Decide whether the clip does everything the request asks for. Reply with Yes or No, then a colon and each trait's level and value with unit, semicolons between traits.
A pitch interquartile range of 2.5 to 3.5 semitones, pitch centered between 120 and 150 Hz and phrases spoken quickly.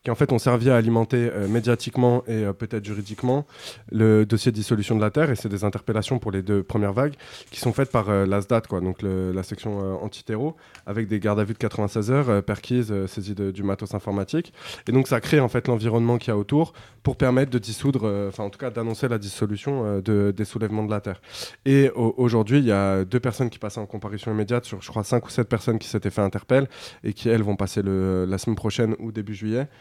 No: average, 3.0 semitones; low, 110 Hz; fast, 250 wpm